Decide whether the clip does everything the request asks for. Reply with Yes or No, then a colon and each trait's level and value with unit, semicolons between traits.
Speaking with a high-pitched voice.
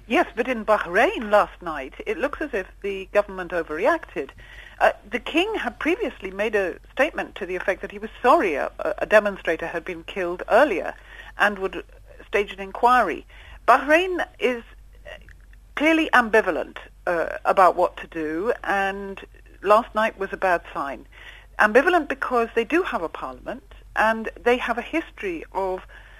Yes: high, 220 Hz